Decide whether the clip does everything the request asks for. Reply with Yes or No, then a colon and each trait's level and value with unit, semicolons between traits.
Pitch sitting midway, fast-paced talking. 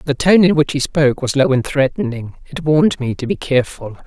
Yes: medium, 145 Hz; fast, 235 wpm